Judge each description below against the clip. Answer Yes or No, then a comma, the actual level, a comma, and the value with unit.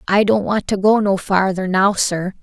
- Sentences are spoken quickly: Yes, fast, 225 wpm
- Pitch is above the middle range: Yes, high, 195 Hz